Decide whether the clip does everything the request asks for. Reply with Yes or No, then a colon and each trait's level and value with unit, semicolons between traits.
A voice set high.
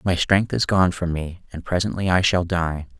No: very low, 90 Hz